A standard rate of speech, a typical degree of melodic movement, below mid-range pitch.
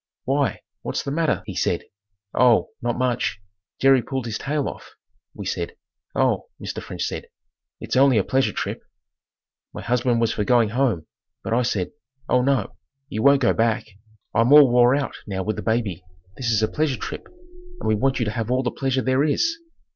Yes: average, 190 wpm; average, 3.4 semitones; low, 125 Hz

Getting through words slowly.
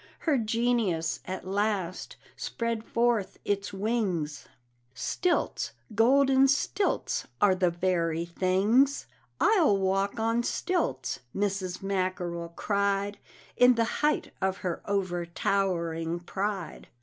Yes: slow, 100 wpm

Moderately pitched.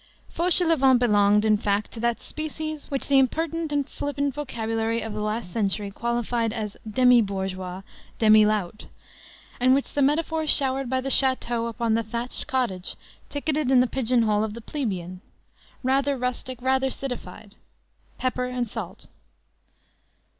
No: high, 245 Hz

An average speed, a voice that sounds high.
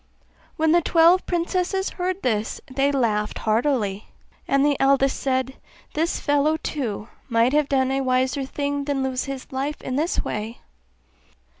Yes: average, 150 wpm; very high, 275 Hz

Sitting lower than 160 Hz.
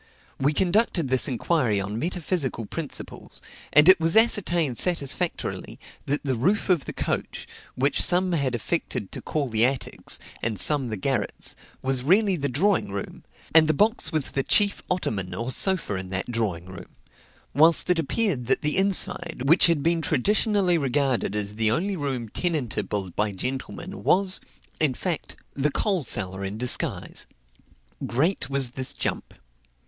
Yes: medium, 140 Hz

